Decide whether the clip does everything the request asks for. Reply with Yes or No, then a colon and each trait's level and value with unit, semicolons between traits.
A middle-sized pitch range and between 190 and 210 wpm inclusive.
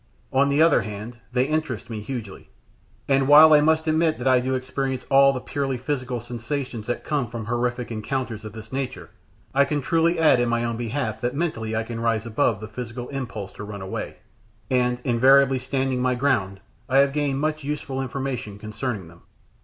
Yes: average, 3.1 semitones; average, 195 wpm